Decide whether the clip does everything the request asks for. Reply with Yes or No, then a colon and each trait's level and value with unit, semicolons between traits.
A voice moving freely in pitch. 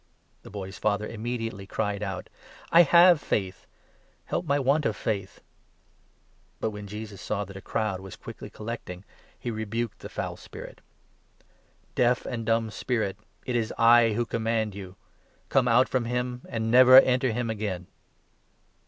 No: average, 3.1 semitones